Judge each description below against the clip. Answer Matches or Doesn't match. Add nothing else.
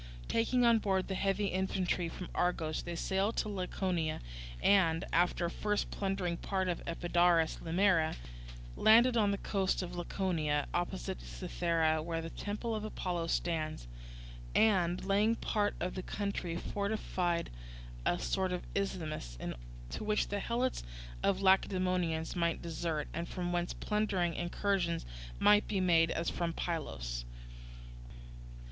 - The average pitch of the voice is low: Doesn't match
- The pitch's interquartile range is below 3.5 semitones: Matches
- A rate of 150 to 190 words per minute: Doesn't match